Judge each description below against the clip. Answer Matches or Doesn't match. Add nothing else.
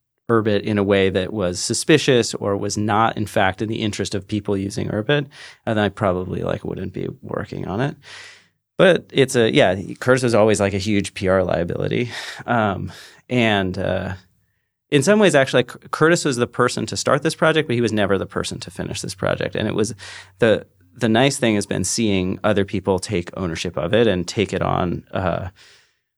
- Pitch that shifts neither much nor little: Matches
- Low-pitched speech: Matches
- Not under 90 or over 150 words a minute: Doesn't match